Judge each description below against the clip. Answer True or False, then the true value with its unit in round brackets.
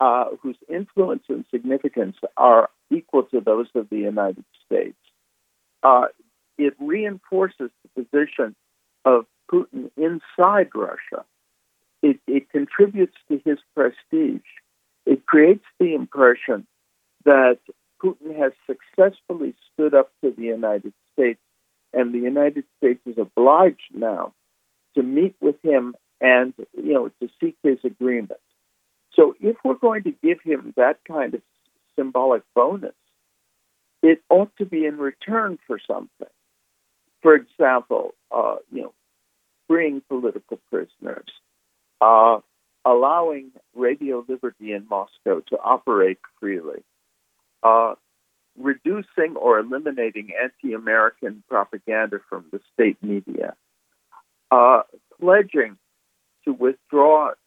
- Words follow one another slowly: True (115 wpm)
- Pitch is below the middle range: False (145 Hz)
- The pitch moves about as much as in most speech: False (8.1 semitones)